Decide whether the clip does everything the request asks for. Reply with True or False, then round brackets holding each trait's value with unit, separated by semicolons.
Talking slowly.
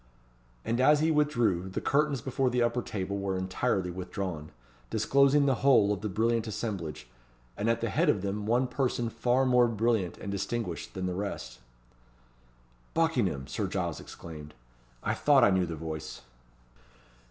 False (160 wpm)